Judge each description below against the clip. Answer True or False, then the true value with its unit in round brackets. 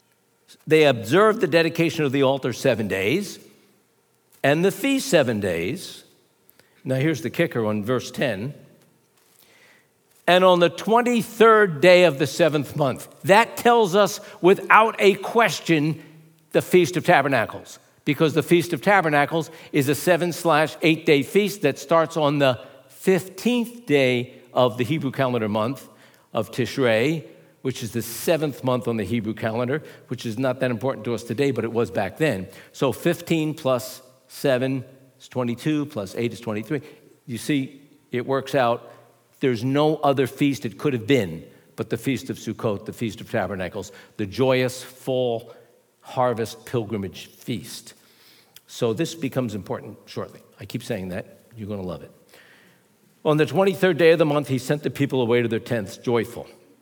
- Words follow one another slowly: False (165 wpm)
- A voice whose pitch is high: False (140 Hz)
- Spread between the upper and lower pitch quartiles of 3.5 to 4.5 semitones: False (5.1 semitones)